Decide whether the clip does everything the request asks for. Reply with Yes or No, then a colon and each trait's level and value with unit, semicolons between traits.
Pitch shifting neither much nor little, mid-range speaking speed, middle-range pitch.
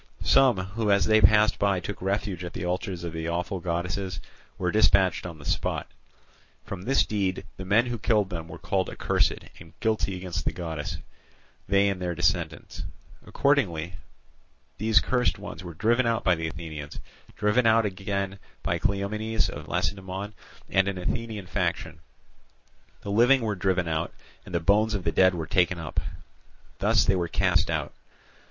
No: average, 3.4 semitones; average, 170 wpm; very low, 95 Hz